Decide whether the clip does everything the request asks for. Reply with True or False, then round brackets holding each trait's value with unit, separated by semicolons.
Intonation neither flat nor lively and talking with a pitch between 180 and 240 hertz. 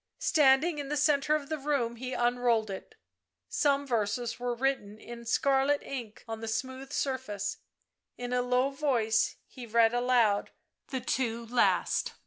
False (3.1 semitones; 250 Hz)